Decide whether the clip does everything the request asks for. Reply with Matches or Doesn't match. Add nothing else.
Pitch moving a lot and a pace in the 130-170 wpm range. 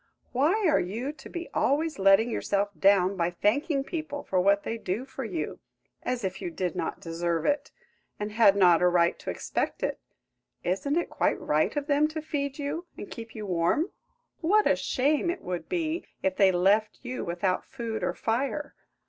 Doesn't match